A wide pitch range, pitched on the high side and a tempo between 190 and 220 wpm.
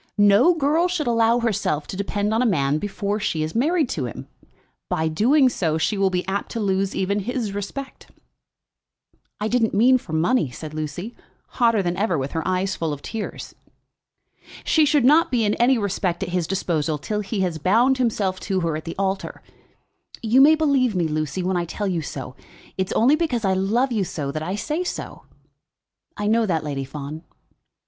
Yes: wide, 6.1 semitones; high, 200 Hz; average, 195 wpm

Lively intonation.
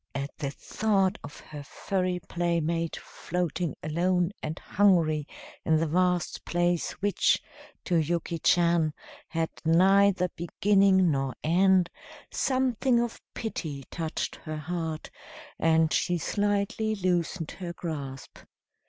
No: average, 3.0 semitones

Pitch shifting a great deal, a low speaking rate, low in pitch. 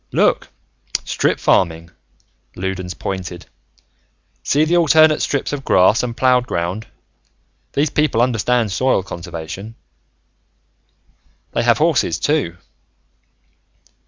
Yes: wide, 6.7 semitones; slow, 100 wpm; low, 110 Hz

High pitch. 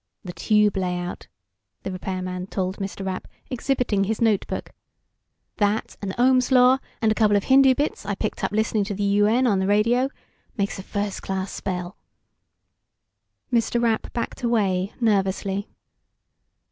Yes: high, 205 Hz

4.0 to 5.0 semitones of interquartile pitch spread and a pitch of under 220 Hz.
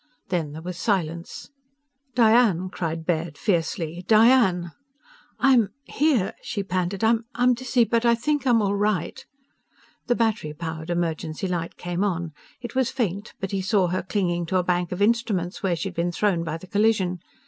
Yes: average, 4.6 semitones; medium, 185 Hz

